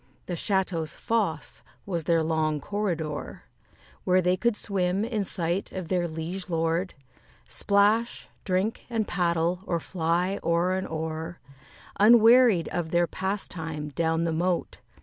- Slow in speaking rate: Yes, slow, 130 wpm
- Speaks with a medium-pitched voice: Yes, medium, 175 Hz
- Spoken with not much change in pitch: No, average, 3.3 semitones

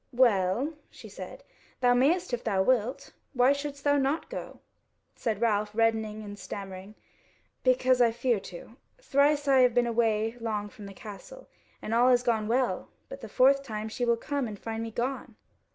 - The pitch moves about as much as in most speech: Yes, average, 3.7 semitones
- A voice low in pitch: No, high, 235 Hz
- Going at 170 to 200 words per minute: Yes, average, 180 wpm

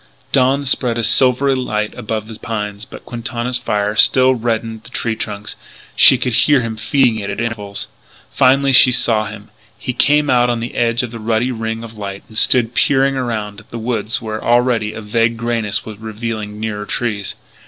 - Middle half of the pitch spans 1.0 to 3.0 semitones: Yes, narrow, 2.5 semitones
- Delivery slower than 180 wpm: No, average, 195 wpm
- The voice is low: Yes, low, 115 Hz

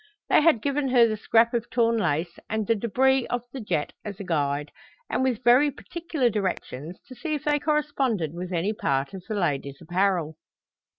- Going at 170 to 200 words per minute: Yes, average, 185 wpm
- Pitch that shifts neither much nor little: No, wide, 7.0 semitones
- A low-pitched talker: No, high, 220 Hz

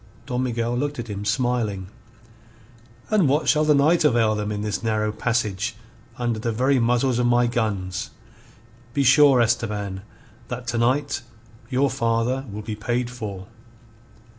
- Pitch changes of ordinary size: Yes, average, 3.3 semitones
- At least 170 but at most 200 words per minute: No, average, 150 wpm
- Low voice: Yes, low, 120 Hz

